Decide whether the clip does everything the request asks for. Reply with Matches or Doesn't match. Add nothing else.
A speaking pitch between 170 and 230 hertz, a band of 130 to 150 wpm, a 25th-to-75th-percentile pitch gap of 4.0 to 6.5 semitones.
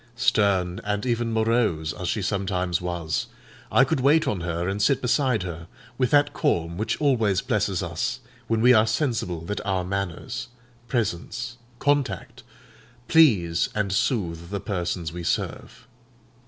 Doesn't match